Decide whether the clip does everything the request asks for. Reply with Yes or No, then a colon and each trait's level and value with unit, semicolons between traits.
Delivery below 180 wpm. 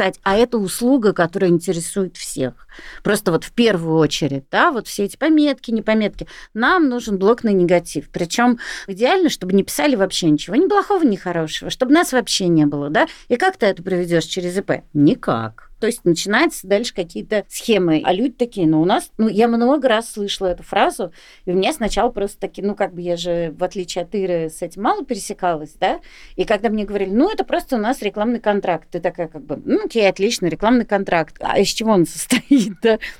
No: fast, 200 wpm